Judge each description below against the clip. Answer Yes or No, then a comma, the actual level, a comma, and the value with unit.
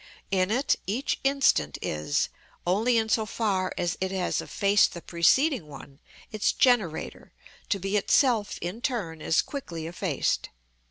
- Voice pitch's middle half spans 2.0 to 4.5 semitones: No, wide, 5.4 semitones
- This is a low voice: No, high, 200 Hz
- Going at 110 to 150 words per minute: Yes, average, 145 wpm